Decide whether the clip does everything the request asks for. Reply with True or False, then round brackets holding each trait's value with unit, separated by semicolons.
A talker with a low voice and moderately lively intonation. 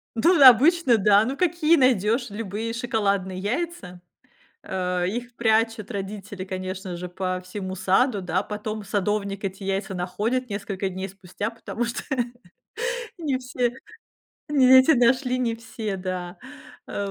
False (210 Hz; 4.4 semitones)